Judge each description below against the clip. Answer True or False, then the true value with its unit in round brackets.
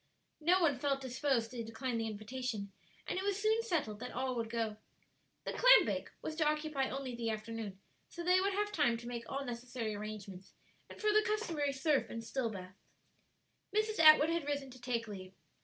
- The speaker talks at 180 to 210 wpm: True (195 wpm)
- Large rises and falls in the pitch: True (5.7 semitones)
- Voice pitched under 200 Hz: False (260 Hz)